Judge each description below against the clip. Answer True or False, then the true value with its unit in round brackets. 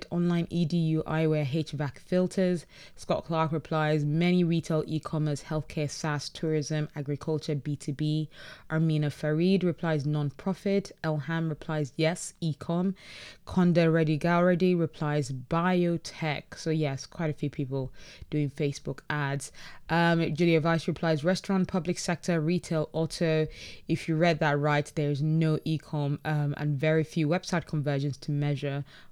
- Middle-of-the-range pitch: True (155 Hz)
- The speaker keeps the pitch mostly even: True (2.2 semitones)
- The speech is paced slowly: True (130 wpm)